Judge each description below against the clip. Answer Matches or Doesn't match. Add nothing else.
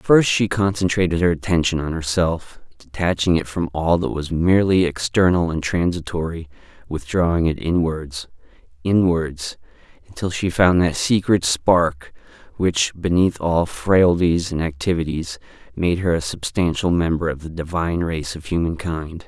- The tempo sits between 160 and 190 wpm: Doesn't match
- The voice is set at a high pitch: Doesn't match